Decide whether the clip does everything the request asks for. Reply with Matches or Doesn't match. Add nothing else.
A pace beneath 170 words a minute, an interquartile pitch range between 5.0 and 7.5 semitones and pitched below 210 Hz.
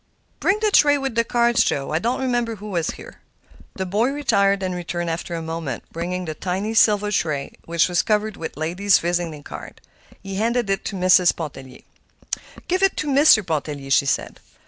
Doesn't match